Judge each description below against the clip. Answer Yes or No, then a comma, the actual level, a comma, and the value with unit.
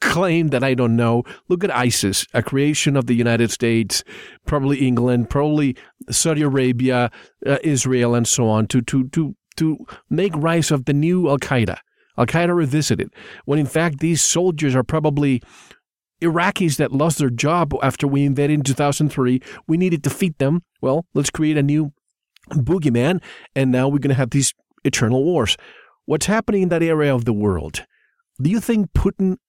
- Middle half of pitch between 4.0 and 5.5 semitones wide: Yes, average, 4.3 semitones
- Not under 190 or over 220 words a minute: No, average, 175 wpm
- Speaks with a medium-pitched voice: Yes, medium, 145 Hz